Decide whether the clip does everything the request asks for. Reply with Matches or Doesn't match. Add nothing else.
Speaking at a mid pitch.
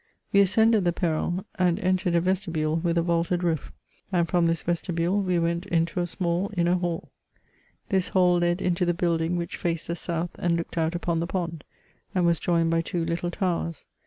Matches